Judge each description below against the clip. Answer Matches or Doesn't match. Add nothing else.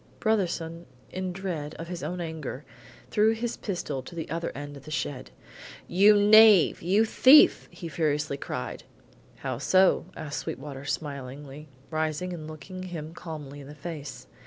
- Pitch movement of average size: Matches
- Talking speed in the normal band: Matches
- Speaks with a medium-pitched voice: Matches